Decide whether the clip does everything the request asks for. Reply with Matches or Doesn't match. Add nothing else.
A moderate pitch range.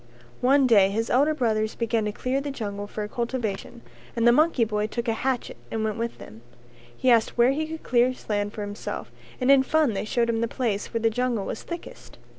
Matches